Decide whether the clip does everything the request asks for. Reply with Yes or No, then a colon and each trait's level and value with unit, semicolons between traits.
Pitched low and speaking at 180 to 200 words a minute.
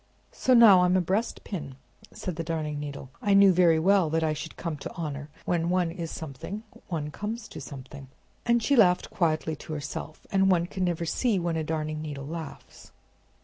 No: medium, 165 Hz; average, 190 wpm